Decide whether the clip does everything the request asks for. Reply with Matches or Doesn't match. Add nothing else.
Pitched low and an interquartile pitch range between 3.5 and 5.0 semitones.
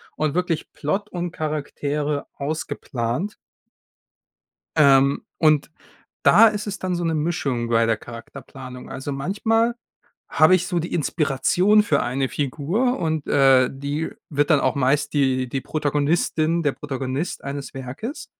Doesn't match